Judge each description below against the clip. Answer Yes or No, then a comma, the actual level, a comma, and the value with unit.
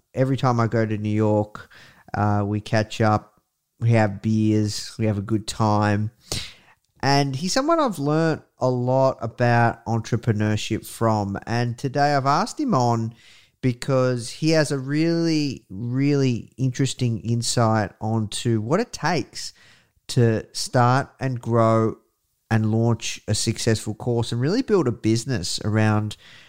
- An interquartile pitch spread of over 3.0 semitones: Yes, average, 3.5 semitones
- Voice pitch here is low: Yes, low, 115 Hz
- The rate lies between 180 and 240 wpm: No, average, 140 wpm